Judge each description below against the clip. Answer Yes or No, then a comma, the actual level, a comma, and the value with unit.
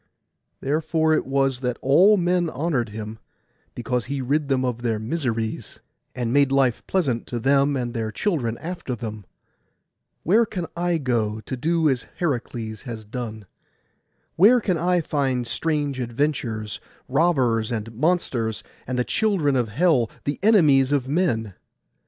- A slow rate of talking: No, average, 145 wpm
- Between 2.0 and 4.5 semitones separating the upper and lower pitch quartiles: No, wide, 5.4 semitones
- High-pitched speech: No, low, 135 Hz